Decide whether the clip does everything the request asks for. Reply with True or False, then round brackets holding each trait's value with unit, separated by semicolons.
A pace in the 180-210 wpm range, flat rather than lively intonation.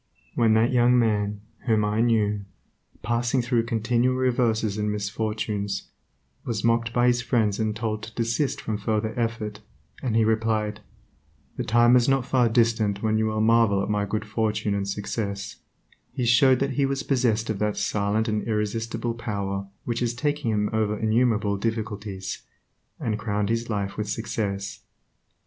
False (165 wpm; 2.0 semitones)